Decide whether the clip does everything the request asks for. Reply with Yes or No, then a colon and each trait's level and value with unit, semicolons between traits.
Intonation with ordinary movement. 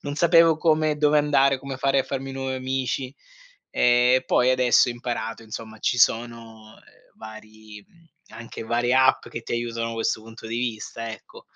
Yes: average, 3.0 semitones